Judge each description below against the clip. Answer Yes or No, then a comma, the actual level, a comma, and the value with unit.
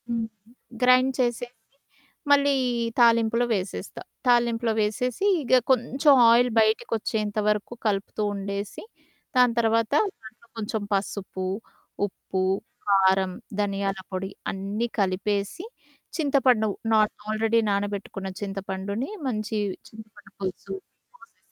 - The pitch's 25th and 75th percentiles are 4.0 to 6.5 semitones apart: No, average, 3.2 semitones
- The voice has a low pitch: No, high, 215 Hz